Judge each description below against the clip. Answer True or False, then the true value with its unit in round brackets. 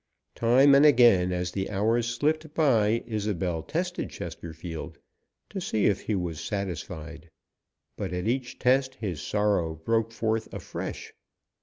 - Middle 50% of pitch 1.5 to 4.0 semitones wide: False (5.6 semitones)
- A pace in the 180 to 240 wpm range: False (135 wpm)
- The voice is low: True (110 Hz)